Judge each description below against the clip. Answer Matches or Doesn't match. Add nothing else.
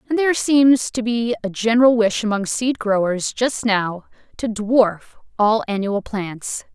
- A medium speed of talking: Matches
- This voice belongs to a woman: Matches